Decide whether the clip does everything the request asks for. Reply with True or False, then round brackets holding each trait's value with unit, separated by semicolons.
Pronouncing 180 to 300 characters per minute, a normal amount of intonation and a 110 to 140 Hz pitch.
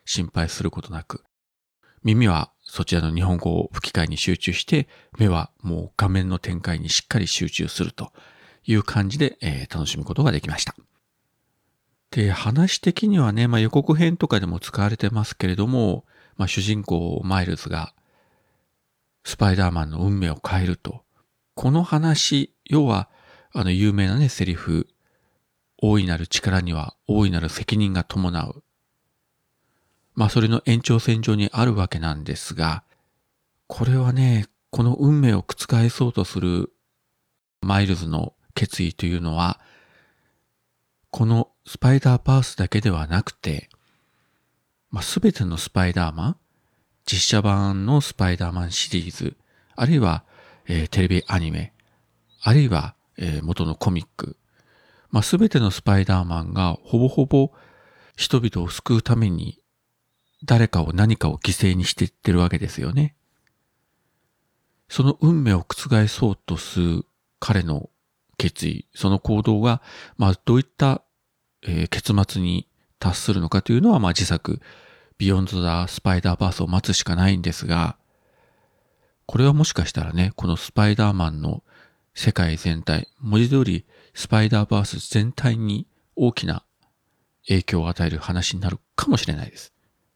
False (285 characters per minute; 4.9 semitones; 100 Hz)